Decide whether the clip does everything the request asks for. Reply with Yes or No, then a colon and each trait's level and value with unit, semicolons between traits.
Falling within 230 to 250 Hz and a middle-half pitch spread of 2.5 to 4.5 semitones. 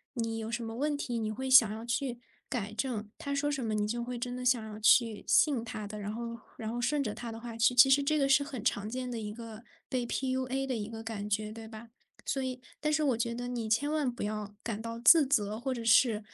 Yes: high, 235 Hz; average, 2.9 semitones